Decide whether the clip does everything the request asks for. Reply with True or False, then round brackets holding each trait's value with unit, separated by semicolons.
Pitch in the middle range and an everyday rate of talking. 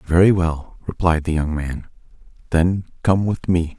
False (85 Hz; 160 wpm)